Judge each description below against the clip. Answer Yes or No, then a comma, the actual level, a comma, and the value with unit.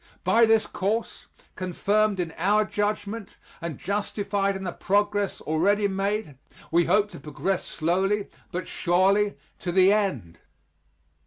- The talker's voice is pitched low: No, high, 200 Hz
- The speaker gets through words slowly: Yes, slow, 130 wpm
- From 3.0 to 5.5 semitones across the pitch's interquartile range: No, narrow, 2.6 semitones